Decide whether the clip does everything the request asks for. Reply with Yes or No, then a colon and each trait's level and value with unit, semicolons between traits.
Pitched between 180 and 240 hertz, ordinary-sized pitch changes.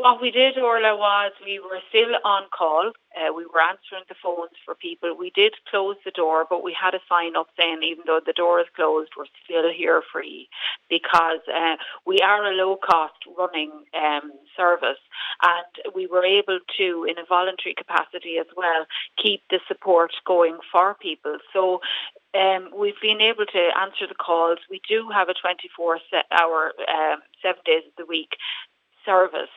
Yes: medium, 185 Hz; average, 3.7 semitones